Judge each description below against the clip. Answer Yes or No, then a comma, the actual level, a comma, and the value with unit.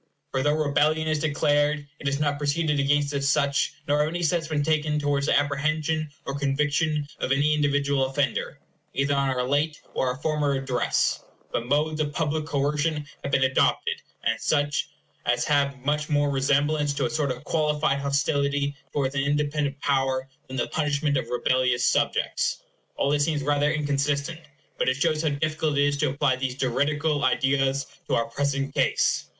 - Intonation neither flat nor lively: No, narrow, 1.4 semitones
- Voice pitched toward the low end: No, medium, 145 Hz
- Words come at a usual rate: Yes, average, 180 wpm